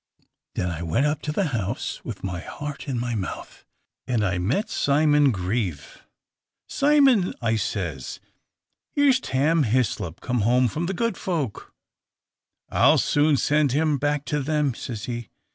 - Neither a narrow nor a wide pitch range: No, wide, 6.1 semitones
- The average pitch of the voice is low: Yes, low, 130 Hz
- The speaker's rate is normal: Yes, average, 155 wpm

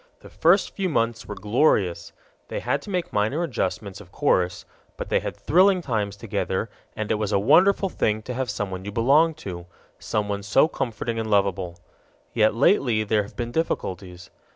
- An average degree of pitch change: No, wide, 6.0 semitones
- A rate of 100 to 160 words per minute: No, average, 175 wpm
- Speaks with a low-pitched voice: Yes, low, 110 Hz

